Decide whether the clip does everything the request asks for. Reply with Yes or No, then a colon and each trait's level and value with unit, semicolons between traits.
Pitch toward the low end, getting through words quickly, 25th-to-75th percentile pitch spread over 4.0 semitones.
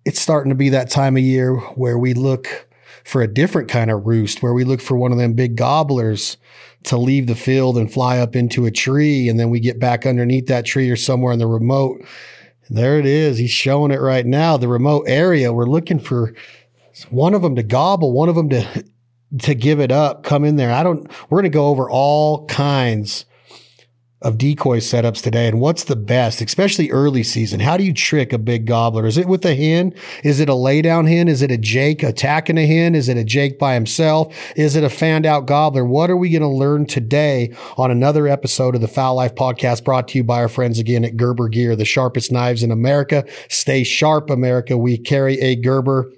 No: low, 130 Hz; fast, 220 wpm; average, 3.3 semitones